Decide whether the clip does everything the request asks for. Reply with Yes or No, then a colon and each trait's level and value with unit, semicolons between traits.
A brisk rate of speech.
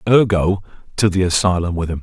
No: average, 180 wpm